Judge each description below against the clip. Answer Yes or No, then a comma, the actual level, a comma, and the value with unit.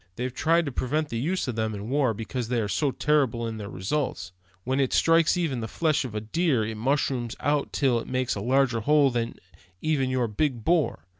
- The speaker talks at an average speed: No, fast, 220 wpm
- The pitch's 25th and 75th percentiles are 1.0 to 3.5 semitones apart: No, average, 4.6 semitones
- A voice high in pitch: No, low, 130 Hz